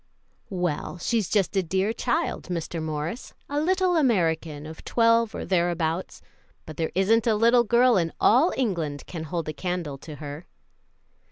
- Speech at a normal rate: Yes, average, 160 wpm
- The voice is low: No, medium, 180 Hz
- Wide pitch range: Yes, wide, 6.2 semitones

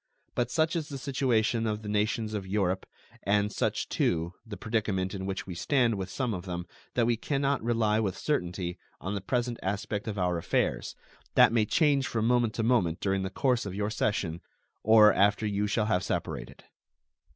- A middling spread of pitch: Yes, average, 3.6 semitones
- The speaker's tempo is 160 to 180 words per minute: No, average, 195 wpm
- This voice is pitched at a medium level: No, low, 105 Hz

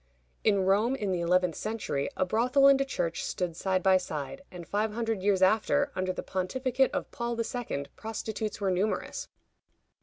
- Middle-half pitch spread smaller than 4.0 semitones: No, average, 4.3 semitones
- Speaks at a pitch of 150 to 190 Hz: No, high, 205 Hz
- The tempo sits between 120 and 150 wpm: No, average, 175 wpm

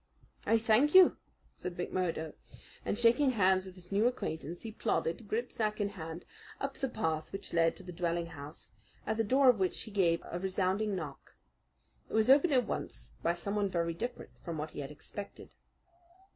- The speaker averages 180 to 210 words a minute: Yes, average, 185 wpm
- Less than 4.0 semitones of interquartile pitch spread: No, average, 4.9 semitones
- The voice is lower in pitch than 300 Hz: Yes, high, 190 Hz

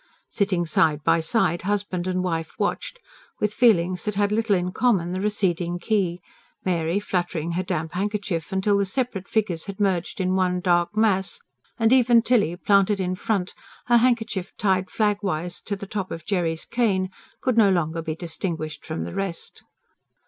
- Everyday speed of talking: Yes, average, 170 wpm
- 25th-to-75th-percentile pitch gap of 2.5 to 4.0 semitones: Yes, average, 3.2 semitones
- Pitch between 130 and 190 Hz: Yes, medium, 185 Hz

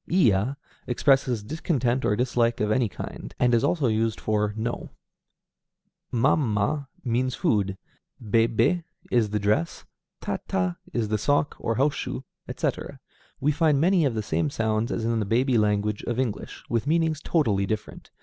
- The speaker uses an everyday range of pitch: Yes, average, 4.4 semitones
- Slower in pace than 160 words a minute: No, average, 165 wpm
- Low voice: Yes, low, 115 Hz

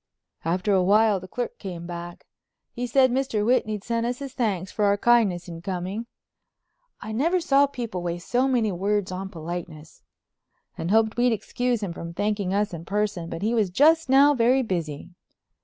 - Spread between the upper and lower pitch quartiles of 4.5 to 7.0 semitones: Yes, average, 5.2 semitones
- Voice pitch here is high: Yes, high, 210 Hz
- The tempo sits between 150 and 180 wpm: Yes, average, 175 wpm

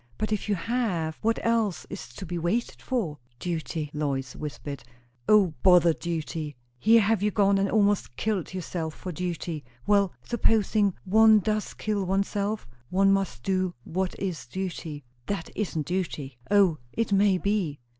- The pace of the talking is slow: No, average, 155 wpm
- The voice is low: No, high, 190 Hz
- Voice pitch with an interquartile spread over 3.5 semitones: Yes, average, 4.2 semitones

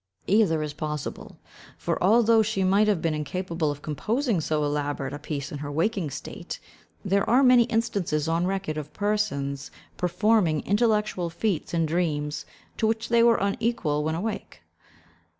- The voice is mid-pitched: Yes, medium, 180 Hz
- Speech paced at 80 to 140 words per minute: No, average, 155 wpm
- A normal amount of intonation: No, wide, 6.0 semitones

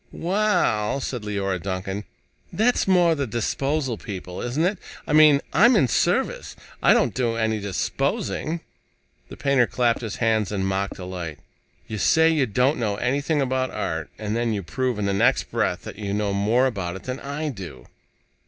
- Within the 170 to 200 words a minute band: Yes, average, 175 wpm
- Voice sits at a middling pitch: No, low, 115 Hz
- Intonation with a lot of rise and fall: Yes, wide, 5.9 semitones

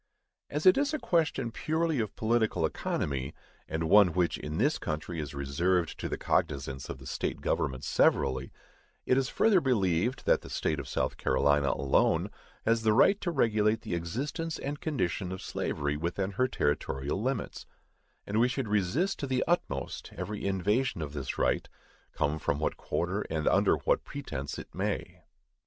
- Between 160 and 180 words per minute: Yes, average, 170 wpm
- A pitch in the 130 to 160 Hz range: No, very low, 95 Hz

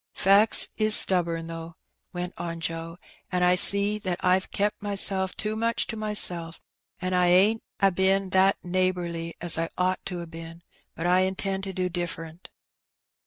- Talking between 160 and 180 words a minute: Yes, average, 165 wpm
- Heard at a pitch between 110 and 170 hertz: No, medium, 185 Hz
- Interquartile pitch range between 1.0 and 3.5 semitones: Yes, narrow, 2.4 semitones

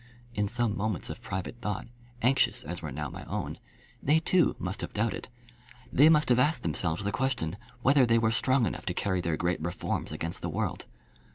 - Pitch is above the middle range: No, low, 110 Hz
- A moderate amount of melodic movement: No, wide, 6.4 semitones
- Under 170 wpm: No, average, 195 wpm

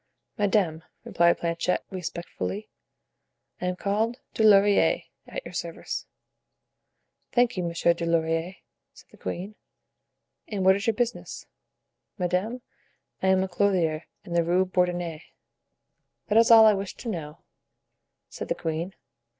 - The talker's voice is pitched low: No, medium, 185 Hz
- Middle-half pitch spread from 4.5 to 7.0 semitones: No, average, 3.3 semitones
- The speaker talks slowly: Yes, slow, 130 wpm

